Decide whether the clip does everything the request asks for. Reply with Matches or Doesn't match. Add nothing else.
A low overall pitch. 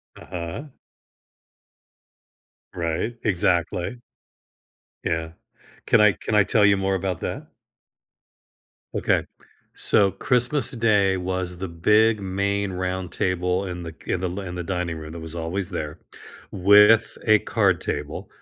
Matches